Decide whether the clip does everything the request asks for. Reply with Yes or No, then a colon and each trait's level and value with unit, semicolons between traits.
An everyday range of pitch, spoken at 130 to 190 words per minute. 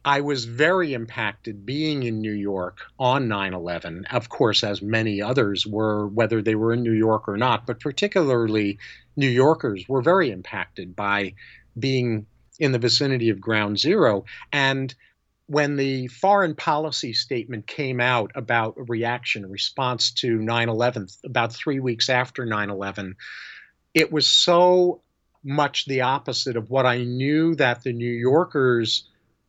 Yes: average, 3.7 semitones; average, 155 wpm